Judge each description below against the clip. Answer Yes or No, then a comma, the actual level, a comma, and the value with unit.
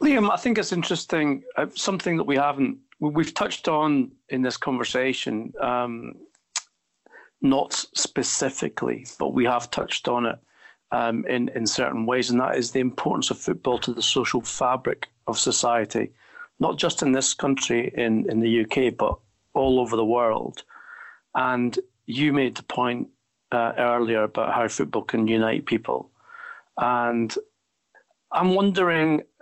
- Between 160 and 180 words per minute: No, average, 145 wpm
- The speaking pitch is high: No, low, 135 Hz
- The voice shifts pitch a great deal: Yes, wide, 7.1 semitones